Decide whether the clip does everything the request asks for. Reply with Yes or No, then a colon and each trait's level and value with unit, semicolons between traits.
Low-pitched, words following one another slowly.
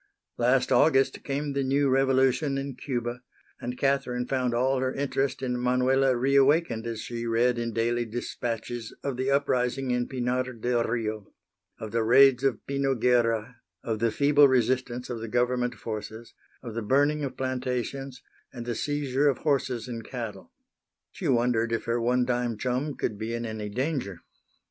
No: low, 125 Hz; average, 165 wpm